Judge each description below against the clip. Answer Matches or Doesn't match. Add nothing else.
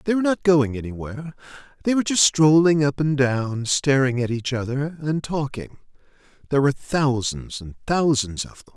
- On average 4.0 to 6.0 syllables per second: Matches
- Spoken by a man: Matches